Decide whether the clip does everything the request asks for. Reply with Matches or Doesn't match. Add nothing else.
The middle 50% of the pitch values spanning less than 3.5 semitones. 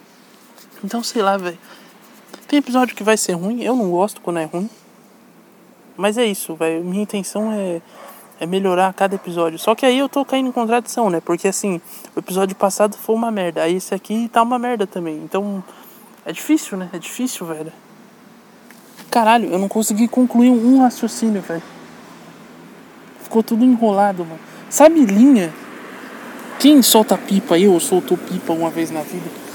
Doesn't match